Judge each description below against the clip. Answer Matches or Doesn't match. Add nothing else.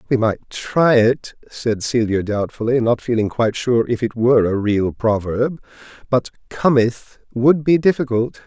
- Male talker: Matches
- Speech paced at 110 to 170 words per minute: Matches